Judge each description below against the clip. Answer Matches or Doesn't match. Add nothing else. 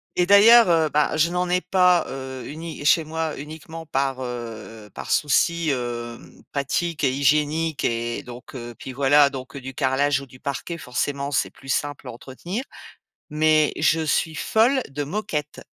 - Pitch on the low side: Doesn't match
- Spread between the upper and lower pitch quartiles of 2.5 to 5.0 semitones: Matches